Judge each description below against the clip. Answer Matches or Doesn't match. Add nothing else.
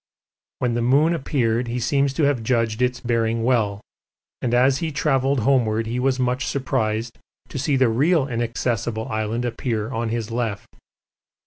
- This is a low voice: Matches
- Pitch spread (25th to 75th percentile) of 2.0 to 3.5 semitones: Matches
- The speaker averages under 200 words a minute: Matches